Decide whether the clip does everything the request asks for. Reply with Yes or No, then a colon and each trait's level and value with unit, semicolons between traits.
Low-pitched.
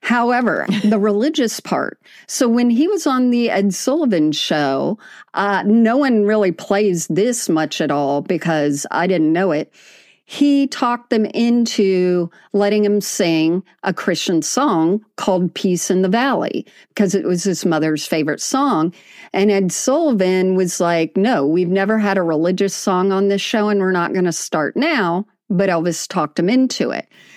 No: high, 195 Hz